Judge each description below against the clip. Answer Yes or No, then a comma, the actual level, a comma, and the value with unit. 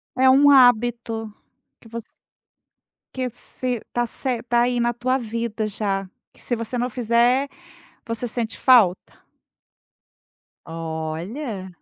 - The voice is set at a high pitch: Yes, high, 235 Hz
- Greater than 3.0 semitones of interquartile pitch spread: No, narrow, 2.6 semitones